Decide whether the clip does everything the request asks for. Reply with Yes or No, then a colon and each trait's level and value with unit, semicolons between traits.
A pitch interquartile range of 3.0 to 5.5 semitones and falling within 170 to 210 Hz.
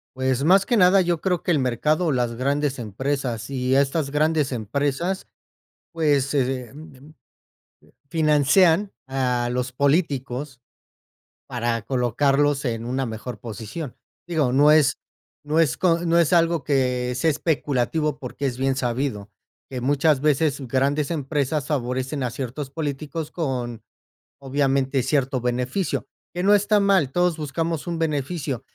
No: average, 3.7 semitones; medium, 140 Hz